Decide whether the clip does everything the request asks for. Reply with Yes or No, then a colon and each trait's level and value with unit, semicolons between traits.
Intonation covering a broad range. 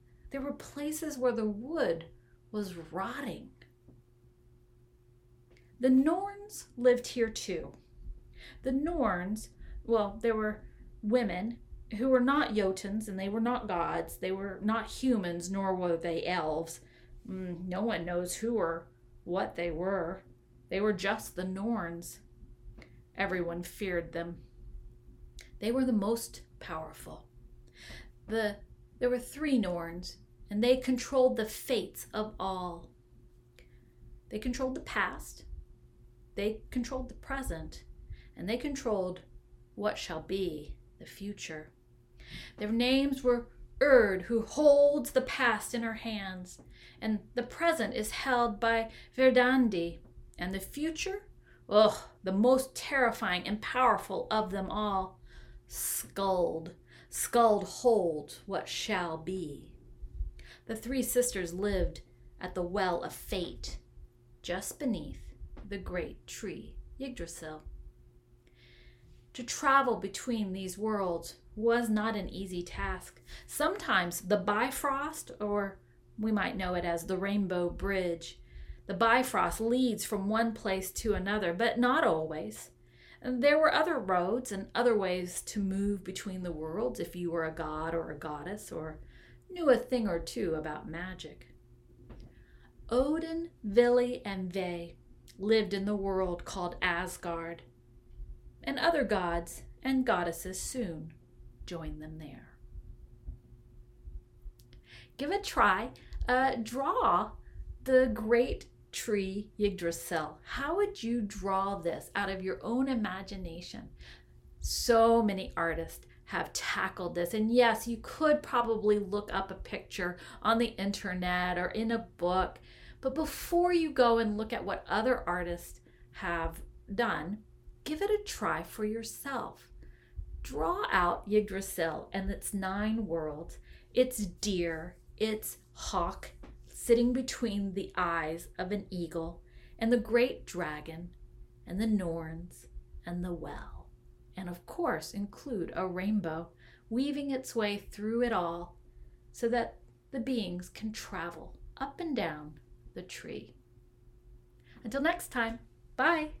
Yes: wide, 6.0 semitones